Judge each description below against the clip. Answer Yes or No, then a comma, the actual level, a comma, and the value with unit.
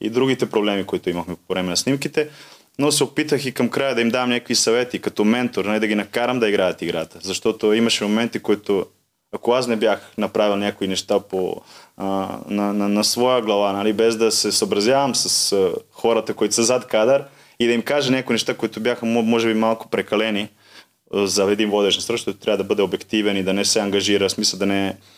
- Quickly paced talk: Yes, fast, 205 wpm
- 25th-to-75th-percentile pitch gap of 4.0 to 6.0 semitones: No, average, 3.3 semitones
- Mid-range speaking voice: No, low, 110 Hz